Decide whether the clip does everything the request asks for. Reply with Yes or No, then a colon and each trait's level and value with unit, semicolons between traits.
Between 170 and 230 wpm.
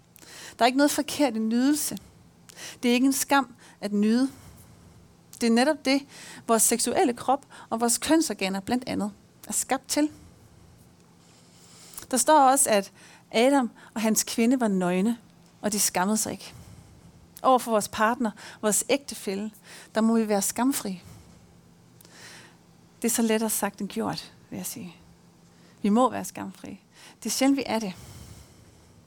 No: average, 155 wpm